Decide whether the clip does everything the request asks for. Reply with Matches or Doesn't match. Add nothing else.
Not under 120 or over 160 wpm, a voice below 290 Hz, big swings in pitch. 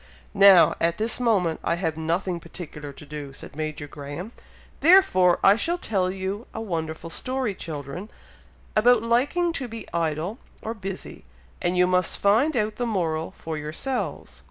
Matches